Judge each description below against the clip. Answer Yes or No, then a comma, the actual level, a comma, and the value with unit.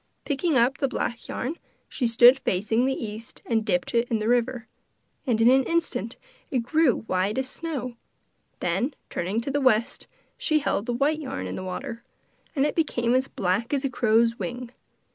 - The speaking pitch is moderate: No, high, 240 Hz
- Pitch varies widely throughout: No, average, 3.2 semitones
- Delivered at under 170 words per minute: No, average, 185 wpm